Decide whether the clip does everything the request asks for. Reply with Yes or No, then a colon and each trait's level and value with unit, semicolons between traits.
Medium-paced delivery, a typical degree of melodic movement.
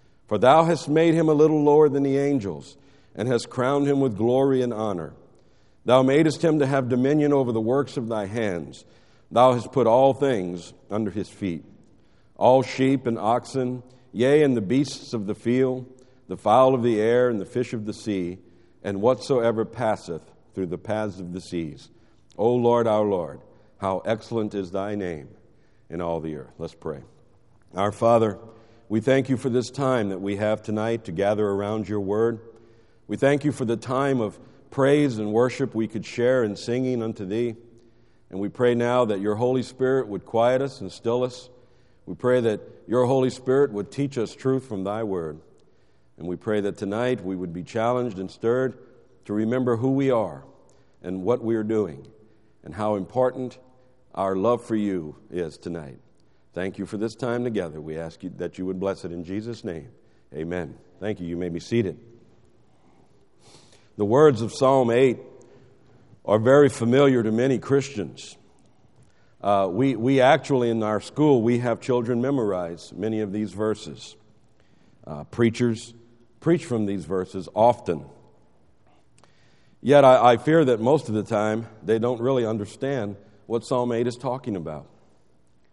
Yes: average, 175 wpm; average, 4.0 semitones